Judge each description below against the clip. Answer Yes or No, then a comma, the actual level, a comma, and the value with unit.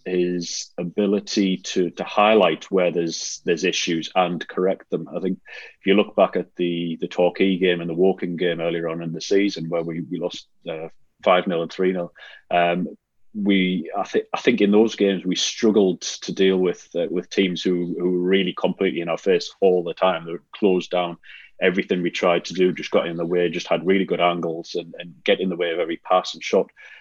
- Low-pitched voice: Yes, very low, 90 Hz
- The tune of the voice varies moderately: No, narrow, 1.7 semitones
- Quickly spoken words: Yes, fast, 220 wpm